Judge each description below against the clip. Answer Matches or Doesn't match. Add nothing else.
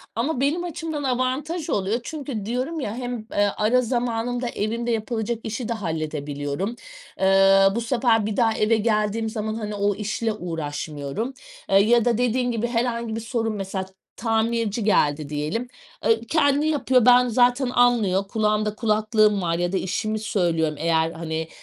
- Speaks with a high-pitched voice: Matches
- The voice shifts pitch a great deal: Doesn't match